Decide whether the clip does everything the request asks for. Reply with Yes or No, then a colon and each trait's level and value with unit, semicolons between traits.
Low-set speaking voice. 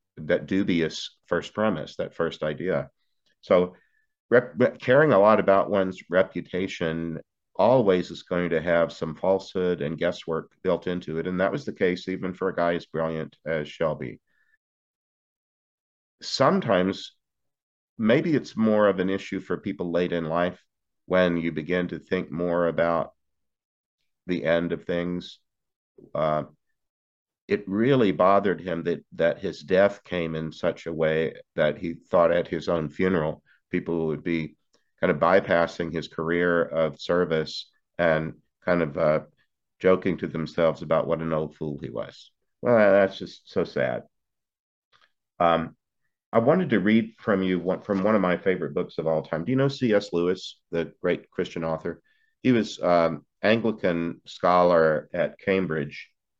Yes: very low, 85 Hz